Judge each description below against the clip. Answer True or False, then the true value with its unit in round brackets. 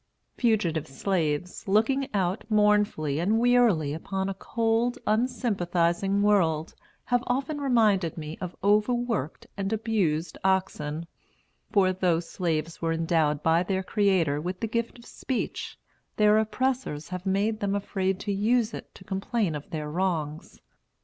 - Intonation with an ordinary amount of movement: True (4.9 semitones)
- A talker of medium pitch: False (195 Hz)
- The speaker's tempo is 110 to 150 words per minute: True (135 wpm)